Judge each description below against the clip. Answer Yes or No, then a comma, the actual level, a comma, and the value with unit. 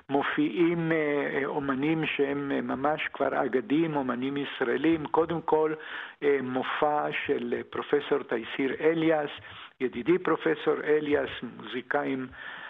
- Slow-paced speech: Yes, slow, 90 wpm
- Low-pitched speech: No, medium, 150 Hz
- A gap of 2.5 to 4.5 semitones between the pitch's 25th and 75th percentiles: Yes, average, 2.9 semitones